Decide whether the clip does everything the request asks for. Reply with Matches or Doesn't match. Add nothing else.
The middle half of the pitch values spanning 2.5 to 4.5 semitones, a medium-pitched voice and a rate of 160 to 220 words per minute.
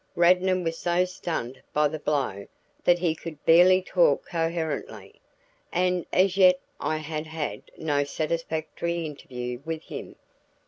Doesn't match